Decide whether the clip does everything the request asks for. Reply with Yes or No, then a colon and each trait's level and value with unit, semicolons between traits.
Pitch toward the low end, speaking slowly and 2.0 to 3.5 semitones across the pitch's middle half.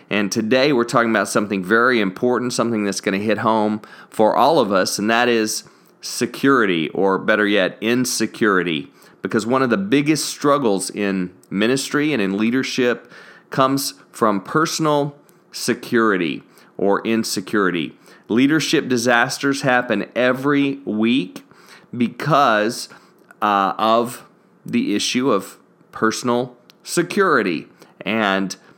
No: low, 120 Hz; slow, 120 wpm; average, 3.9 semitones